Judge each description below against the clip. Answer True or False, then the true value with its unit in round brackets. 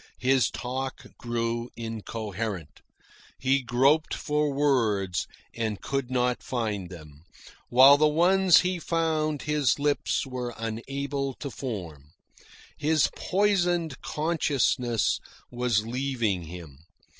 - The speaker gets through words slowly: True (105 wpm)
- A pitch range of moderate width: True (4.8 semitones)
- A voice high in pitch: False (125 Hz)